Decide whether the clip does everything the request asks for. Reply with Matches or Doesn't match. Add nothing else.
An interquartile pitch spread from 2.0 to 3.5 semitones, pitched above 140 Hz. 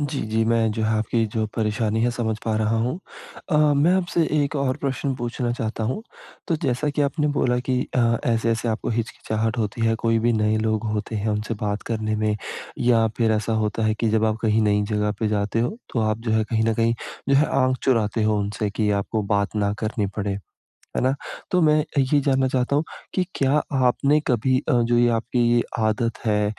Doesn't match